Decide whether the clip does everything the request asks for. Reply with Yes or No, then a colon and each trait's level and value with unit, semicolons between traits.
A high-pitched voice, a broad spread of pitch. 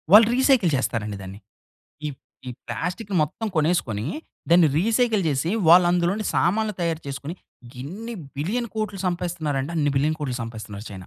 No: medium, 170 Hz; wide, 7.2 semitones